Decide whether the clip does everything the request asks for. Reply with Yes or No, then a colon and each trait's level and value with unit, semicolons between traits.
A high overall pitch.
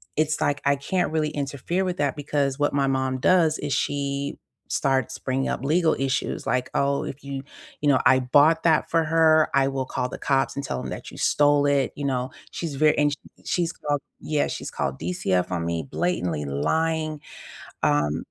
No: medium, 140 Hz